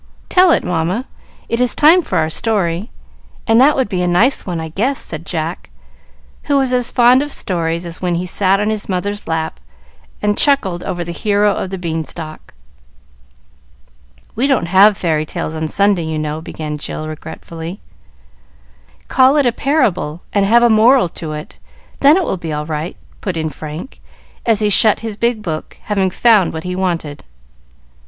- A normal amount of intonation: No, wide, 6.0 semitones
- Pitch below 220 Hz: Yes, medium, 185 Hz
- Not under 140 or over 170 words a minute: No, average, 180 wpm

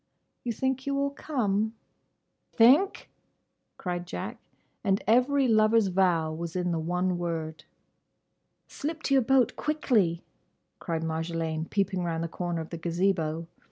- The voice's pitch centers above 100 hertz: Yes, medium, 185 Hz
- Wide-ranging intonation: Yes, wide, 6.7 semitones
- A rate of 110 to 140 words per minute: Yes, slow, 135 wpm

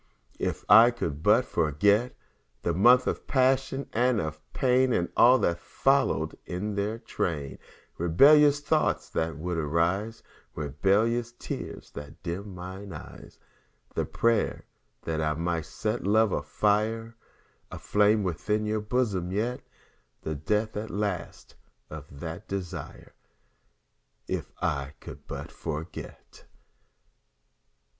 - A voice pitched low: Yes, low, 100 Hz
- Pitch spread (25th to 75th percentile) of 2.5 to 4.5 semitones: No, wide, 5.6 semitones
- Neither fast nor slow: No, slow, 120 wpm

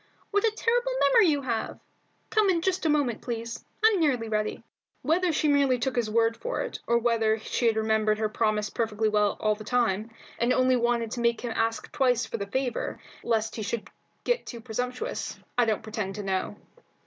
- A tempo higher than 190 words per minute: Yes, average, 200 wpm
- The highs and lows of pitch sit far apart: No, average, 3.9 semitones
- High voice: Yes, high, 235 Hz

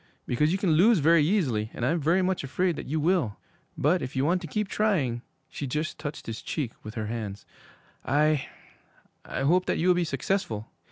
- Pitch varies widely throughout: Yes, wide, 6.1 semitones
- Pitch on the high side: No, medium, 155 Hz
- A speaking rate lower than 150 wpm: No, fast, 205 wpm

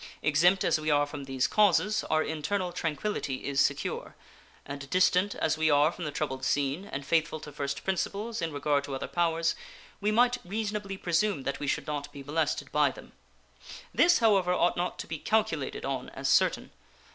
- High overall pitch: No, medium, 160 Hz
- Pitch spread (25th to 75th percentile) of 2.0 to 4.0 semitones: No, average, 5.1 semitones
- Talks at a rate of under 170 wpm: No, average, 185 wpm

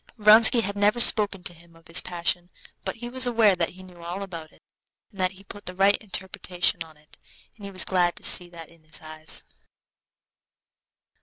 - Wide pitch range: No, average, 3.2 semitones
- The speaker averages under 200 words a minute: No, fast, 205 wpm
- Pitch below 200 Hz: Yes, medium, 185 Hz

